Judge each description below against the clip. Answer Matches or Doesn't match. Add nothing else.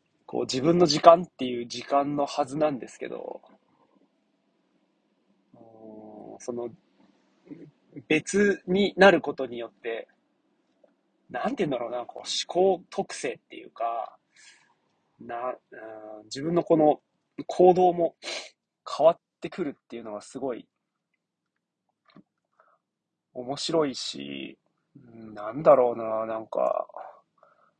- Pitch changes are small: Doesn't match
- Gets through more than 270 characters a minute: Doesn't match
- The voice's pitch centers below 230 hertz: Matches